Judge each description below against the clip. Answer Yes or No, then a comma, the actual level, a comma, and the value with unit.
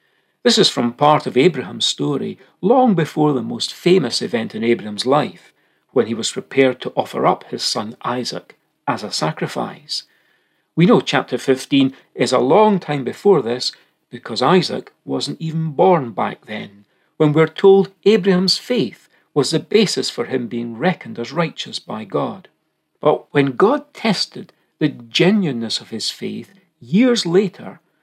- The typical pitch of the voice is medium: Yes, medium, 155 Hz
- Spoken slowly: No, average, 155 wpm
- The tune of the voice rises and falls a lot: Yes, wide, 7.5 semitones